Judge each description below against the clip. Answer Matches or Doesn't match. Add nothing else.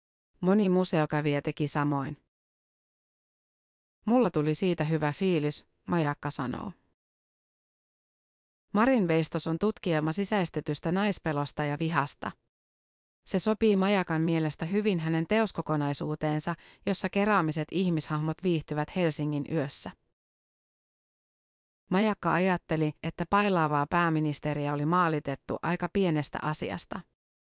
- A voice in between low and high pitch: Matches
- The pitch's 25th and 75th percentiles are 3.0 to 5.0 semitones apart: Matches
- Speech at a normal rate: Doesn't match